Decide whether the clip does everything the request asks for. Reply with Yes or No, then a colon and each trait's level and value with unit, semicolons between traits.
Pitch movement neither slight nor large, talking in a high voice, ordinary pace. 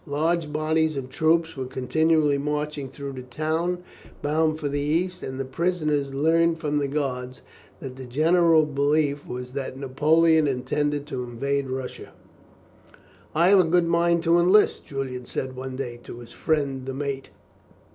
No: average, 3.3 semitones; medium, 145 Hz; average, 160 wpm